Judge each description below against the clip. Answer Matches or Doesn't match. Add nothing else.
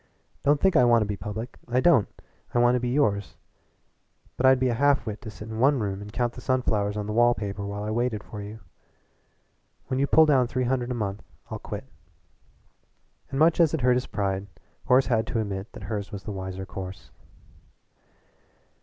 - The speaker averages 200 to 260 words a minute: Matches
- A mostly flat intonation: Doesn't match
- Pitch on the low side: Matches